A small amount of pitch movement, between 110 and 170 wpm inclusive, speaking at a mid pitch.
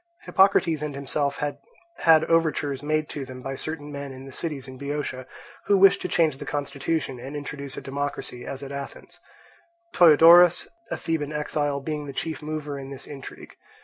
No: narrow, 2.2 semitones; average, 180 wpm; medium, 145 Hz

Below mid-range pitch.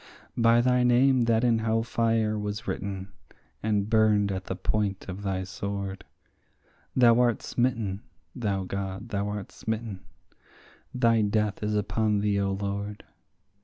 Yes: low, 105 Hz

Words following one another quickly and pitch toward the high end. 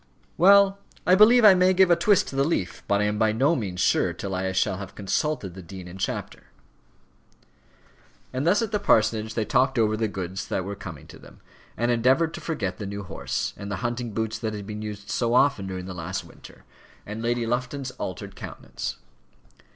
No: fast, 210 wpm; low, 110 Hz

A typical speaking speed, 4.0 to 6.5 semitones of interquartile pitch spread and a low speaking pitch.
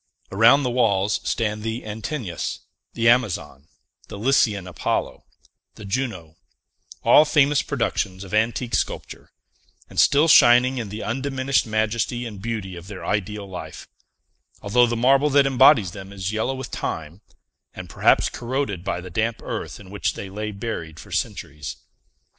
Yes: average, 150 wpm; average, 4.4 semitones; low, 110 Hz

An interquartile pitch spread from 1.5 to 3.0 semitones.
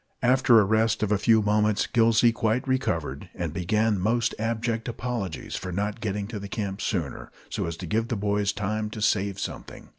Yes: narrow, 2.5 semitones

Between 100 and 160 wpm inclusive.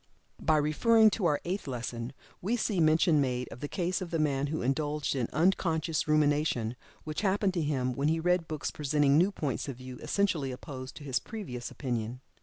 No: average, 195 wpm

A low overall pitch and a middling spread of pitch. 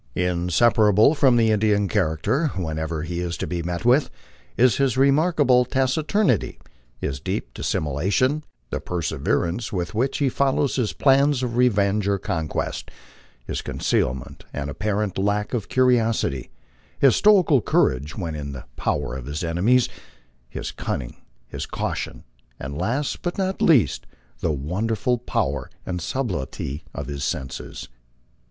No: low, 105 Hz; wide, 7.9 semitones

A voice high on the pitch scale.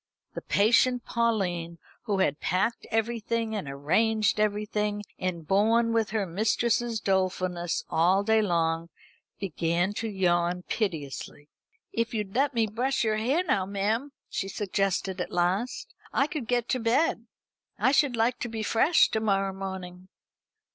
Yes: high, 210 Hz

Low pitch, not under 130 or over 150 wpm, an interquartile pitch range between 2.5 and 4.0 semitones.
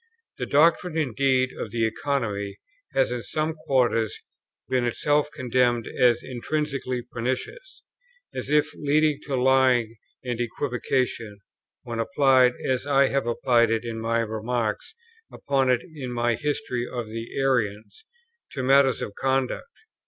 Yes: low, 125 Hz; slow, 135 wpm; average, 2.9 semitones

